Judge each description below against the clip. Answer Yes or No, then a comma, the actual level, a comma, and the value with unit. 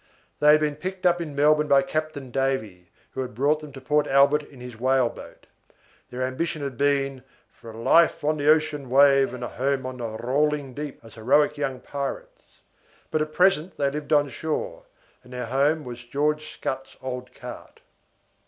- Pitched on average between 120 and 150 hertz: Yes, medium, 140 Hz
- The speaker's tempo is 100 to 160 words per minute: No, average, 185 wpm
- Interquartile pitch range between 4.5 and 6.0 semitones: No, average, 2.8 semitones